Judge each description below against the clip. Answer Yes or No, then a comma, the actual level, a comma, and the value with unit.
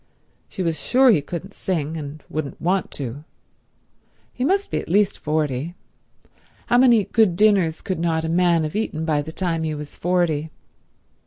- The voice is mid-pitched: Yes, medium, 165 Hz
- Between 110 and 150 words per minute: No, average, 170 wpm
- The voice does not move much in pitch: No, average, 3.8 semitones